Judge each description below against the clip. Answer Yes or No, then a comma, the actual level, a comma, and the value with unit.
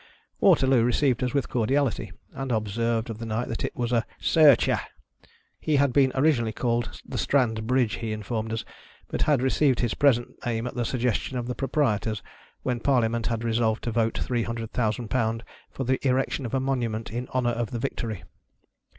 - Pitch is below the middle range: Yes, low, 120 Hz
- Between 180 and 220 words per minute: Yes, average, 190 wpm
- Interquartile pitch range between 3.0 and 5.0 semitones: No, narrow, 2.5 semitones